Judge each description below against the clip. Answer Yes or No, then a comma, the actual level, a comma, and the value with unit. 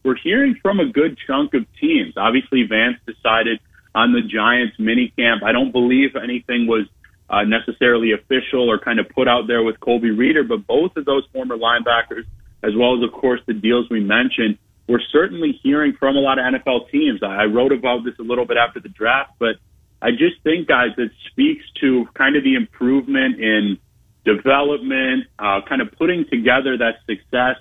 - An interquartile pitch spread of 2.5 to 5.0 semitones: Yes, average, 2.9 semitones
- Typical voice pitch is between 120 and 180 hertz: Yes, low, 125 Hz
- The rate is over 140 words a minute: Yes, average, 195 wpm